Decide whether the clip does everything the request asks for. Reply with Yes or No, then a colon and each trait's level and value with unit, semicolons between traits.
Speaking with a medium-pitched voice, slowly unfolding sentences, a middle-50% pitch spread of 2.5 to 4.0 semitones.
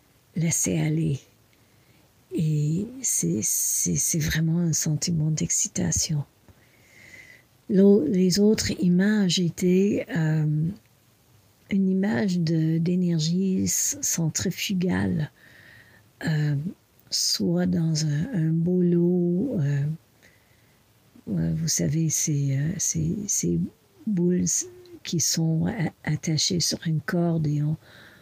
Yes: medium, 165 Hz; slow, 85 wpm; average, 3.3 semitones